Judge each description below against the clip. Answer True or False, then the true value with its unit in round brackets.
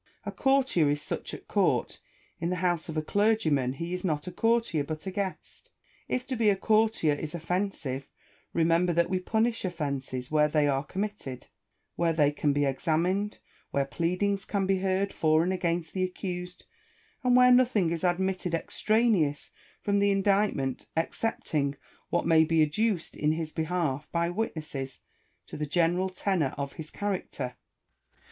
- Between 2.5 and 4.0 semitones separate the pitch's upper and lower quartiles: False (4.4 semitones)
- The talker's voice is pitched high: False (175 Hz)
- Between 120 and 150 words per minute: False (165 wpm)